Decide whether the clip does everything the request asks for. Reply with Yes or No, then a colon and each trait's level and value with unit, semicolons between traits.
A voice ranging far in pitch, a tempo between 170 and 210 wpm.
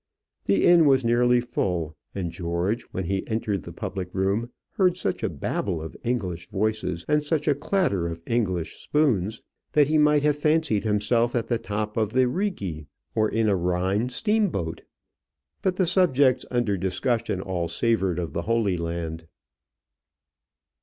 No: wide, 6.3 semitones; average, 160 wpm